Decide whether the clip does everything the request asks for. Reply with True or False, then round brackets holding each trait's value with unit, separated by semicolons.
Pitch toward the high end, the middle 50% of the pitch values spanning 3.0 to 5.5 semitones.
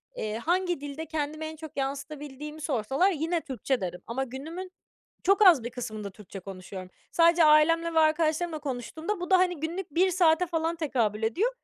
True (310 Hz; 4.4 semitones)